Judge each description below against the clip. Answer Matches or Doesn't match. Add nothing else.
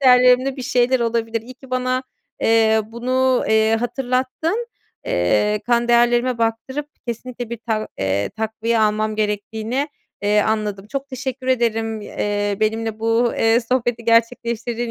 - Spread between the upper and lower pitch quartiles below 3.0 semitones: Matches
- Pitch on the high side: Matches